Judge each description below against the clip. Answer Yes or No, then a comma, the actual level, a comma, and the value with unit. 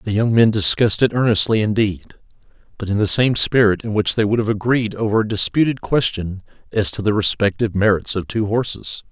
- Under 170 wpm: No, average, 195 wpm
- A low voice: Yes, low, 110 Hz